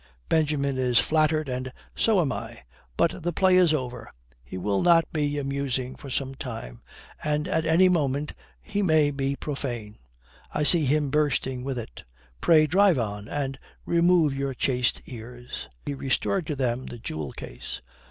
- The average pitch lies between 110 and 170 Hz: Yes, medium, 140 Hz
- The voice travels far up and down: No, average, 3.7 semitones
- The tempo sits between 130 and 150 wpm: No, average, 160 wpm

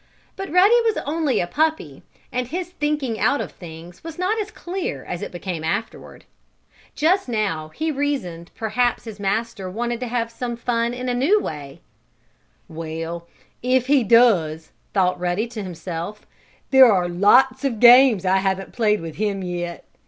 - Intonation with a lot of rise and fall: Yes, wide, 7.0 semitones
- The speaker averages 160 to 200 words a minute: Yes, average, 165 wpm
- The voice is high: Yes, high, 230 Hz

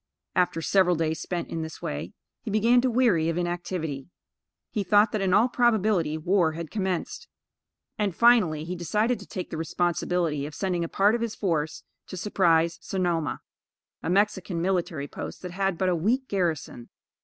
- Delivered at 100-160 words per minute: No, average, 175 wpm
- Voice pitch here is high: No, medium, 180 Hz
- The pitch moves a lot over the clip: No, average, 3.9 semitones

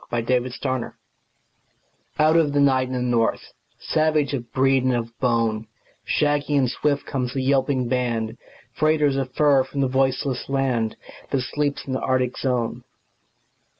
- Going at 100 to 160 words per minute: Yes, average, 155 wpm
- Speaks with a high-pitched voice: No, low, 130 Hz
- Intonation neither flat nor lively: No, narrow, 2.3 semitones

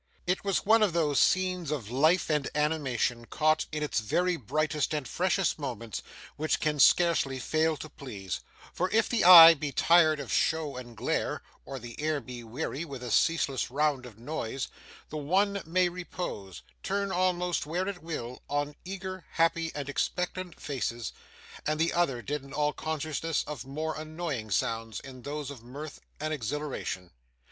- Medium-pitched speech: Yes, medium, 150 Hz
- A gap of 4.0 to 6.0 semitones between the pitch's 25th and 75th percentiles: Yes, average, 4.4 semitones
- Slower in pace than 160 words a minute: No, average, 165 wpm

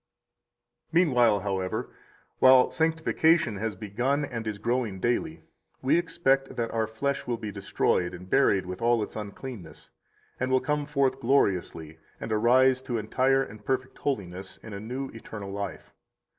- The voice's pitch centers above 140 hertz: No, low, 115 Hz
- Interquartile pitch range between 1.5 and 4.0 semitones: No, average, 4.9 semitones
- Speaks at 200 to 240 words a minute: No, average, 155 wpm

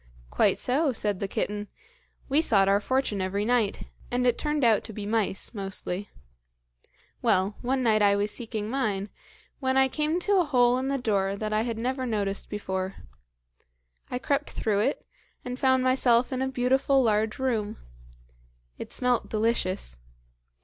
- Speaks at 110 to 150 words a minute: No, average, 165 wpm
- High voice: Yes, high, 230 Hz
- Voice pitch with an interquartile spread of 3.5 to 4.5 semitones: Yes, average, 4.1 semitones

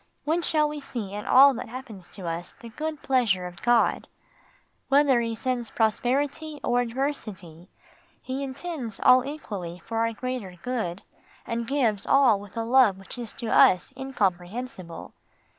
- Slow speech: No, average, 155 wpm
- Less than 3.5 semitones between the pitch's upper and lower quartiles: No, average, 5.0 semitones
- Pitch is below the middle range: No, high, 235 Hz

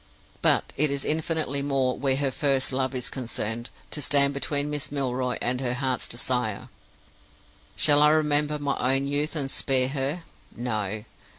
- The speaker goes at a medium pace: Yes, average, 160 wpm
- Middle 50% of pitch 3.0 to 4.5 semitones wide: No, narrow, 2.4 semitones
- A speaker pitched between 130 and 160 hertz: Yes, low, 135 Hz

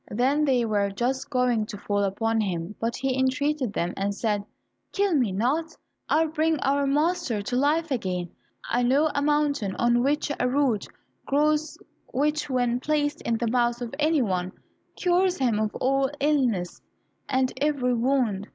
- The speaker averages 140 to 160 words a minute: No, average, 170 wpm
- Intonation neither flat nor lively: Yes, average, 4.8 semitones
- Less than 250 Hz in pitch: No, very high, 255 Hz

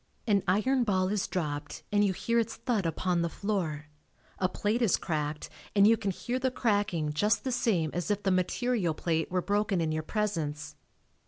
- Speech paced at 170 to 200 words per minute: Yes, average, 190 wpm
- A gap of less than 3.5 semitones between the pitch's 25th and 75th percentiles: No, average, 4.6 semitones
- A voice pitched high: Yes, high, 195 Hz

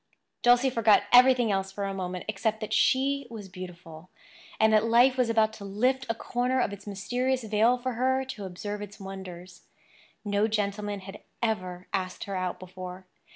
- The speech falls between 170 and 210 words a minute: Yes, average, 175 wpm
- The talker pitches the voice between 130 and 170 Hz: No, high, 210 Hz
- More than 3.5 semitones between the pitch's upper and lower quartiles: Yes, average, 4.1 semitones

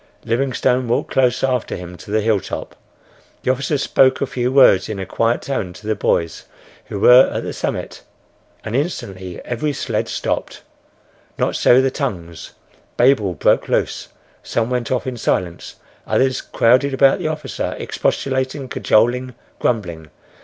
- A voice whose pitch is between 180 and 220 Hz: No, low, 125 Hz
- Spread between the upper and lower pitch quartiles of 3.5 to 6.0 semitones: Yes, average, 4.4 semitones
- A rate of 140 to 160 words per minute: Yes, average, 150 wpm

